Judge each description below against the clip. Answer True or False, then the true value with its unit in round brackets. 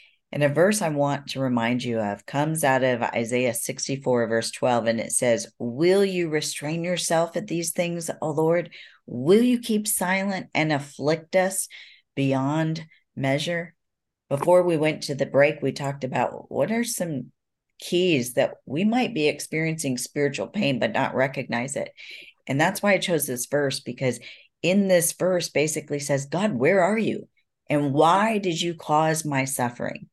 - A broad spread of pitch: False (4.5 semitones)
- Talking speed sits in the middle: True (170 wpm)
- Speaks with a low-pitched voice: False (150 Hz)